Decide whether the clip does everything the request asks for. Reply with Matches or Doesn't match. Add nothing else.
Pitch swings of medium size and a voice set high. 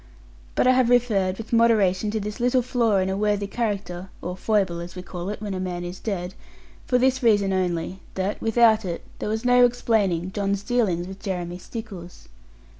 Matches